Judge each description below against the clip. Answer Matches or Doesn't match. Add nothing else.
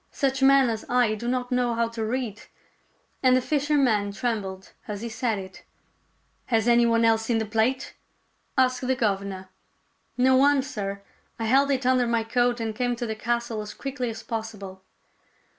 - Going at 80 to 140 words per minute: Doesn't match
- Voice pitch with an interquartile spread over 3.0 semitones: Doesn't match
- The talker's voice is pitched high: Matches